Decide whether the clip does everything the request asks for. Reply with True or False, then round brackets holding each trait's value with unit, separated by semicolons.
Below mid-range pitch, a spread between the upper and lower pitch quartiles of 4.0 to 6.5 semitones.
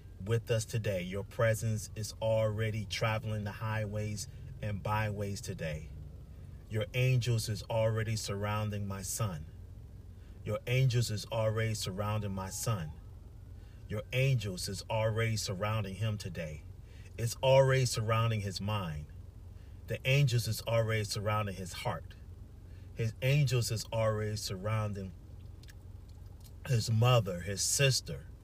False (105 Hz; 2.7 semitones)